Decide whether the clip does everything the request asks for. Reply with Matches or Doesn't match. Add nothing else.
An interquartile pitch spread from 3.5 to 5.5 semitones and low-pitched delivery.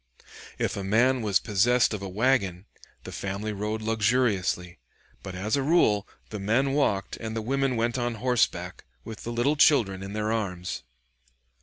Matches